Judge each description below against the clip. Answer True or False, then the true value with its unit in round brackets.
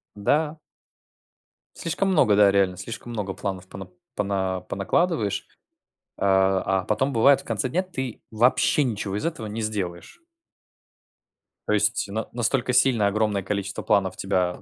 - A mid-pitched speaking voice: False (105 Hz)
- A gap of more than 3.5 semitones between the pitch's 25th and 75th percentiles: True (4.1 semitones)